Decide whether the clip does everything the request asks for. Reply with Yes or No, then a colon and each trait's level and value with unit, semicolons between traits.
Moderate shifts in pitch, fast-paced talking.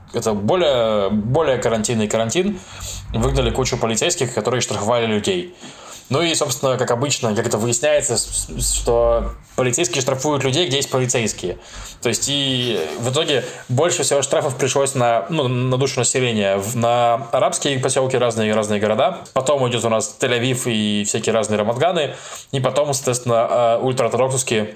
No: average, 3.2 semitones; average, 145 wpm